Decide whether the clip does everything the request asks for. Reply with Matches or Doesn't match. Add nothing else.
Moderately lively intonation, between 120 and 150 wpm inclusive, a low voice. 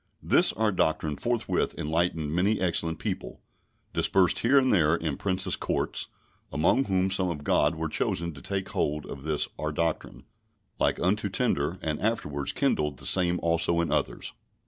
Doesn't match